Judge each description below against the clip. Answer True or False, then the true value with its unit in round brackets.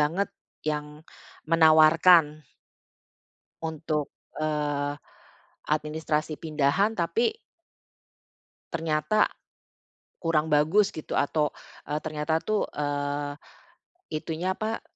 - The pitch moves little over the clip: True (1.8 semitones)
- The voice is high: False (155 Hz)